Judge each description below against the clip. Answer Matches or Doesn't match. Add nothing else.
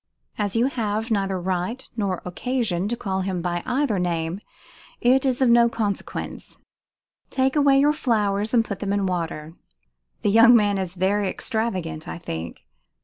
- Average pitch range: Matches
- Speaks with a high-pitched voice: Matches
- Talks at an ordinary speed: Matches